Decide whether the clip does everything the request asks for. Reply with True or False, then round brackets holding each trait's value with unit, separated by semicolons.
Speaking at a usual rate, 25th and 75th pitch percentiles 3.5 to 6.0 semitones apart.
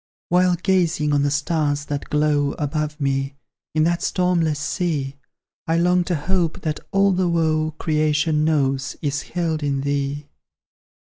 False (145 wpm; 2.9 semitones)